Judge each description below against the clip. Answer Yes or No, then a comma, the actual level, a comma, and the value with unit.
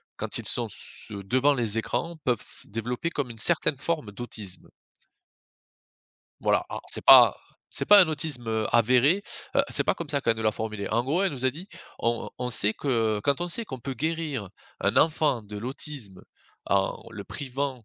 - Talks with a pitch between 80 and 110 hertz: No, low, 125 Hz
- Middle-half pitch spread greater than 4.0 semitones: Yes, average, 5.1 semitones